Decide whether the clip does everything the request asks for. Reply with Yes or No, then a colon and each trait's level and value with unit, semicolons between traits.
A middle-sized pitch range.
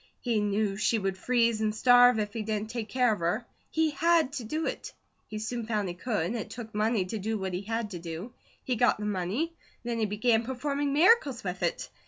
Yes: average, 3.1 semitones